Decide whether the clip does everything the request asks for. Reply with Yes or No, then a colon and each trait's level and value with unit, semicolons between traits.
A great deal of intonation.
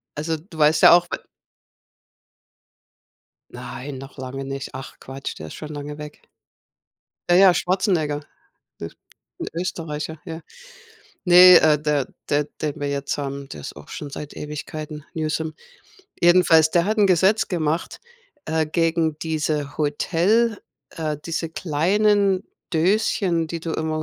No: average, 2.9 semitones